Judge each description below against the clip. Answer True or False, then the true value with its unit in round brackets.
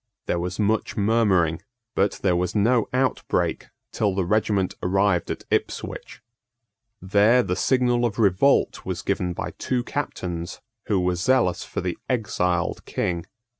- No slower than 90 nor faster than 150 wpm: True (140 wpm)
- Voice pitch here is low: True (100 Hz)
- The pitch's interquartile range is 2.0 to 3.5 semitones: False (4.3 semitones)